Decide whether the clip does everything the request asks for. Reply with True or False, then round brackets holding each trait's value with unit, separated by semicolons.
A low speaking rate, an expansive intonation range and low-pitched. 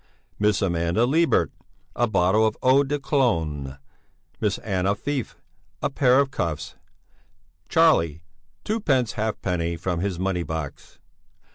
True (120 wpm; 7.7 semitones; 105 Hz)